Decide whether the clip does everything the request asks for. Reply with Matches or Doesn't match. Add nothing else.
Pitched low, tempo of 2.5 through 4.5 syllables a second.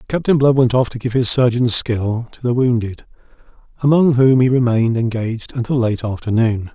Doesn't match